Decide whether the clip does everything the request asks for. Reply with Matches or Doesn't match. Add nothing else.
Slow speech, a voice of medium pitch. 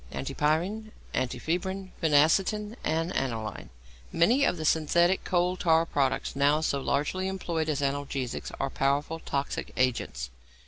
Matches